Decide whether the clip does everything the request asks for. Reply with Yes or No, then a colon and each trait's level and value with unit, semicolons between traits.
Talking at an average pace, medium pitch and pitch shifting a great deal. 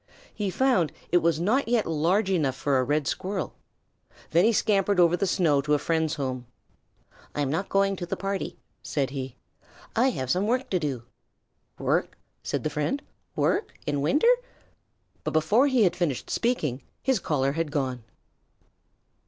Yes: average, 165 wpm; medium, 170 Hz; wide, 5.7 semitones